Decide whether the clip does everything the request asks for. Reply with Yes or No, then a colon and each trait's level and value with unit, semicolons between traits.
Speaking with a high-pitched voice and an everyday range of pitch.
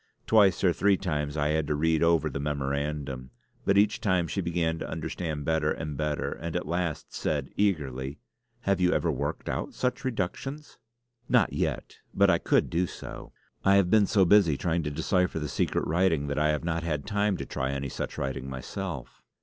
No: very low, 80 Hz; average, 4.4 semitones